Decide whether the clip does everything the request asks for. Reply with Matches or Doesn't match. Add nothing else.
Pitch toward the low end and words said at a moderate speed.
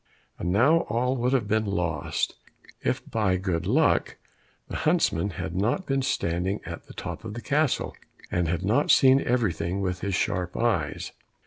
Matches